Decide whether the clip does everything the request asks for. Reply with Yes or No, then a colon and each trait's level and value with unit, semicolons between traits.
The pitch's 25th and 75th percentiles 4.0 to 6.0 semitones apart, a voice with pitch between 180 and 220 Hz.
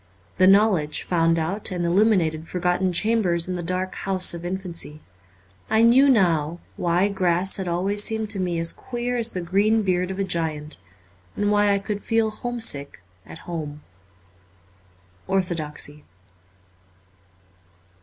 No: average, 3.6 semitones; medium, 185 Hz